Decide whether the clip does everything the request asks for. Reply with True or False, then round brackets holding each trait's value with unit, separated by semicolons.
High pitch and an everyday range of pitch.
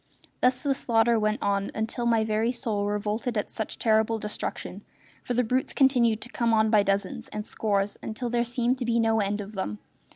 False (220 Hz; 2.2 semitones)